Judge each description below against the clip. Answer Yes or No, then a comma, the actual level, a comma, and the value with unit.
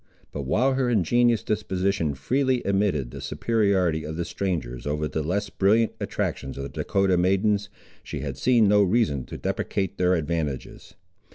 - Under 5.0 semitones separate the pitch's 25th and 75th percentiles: No, wide, 5.5 semitones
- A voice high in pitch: No, very low, 95 Hz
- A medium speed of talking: Yes, average, 160 wpm